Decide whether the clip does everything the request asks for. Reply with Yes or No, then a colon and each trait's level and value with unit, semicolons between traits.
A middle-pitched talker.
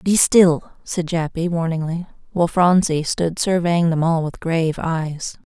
Yes: medium, 165 Hz